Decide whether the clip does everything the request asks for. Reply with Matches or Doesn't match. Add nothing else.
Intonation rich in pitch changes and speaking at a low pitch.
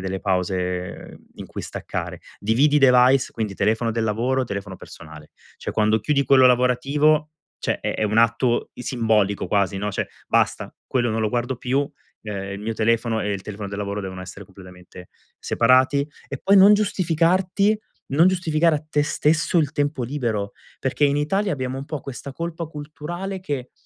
Matches